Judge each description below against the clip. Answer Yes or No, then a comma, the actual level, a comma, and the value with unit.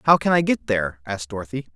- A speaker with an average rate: No, fast, 240 wpm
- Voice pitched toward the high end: No, low, 120 Hz